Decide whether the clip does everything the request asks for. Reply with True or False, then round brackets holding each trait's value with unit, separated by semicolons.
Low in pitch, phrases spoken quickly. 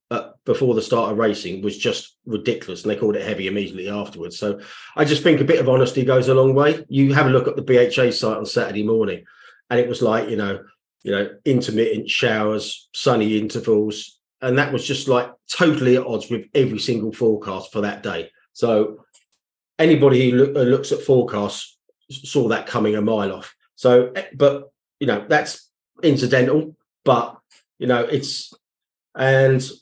False (125 Hz; 180 wpm)